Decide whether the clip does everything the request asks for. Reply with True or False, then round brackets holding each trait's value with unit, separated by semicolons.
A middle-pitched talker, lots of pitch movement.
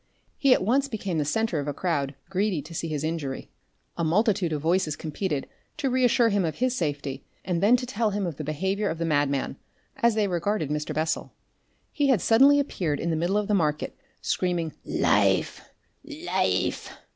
True (180 Hz; 6.1 semitones)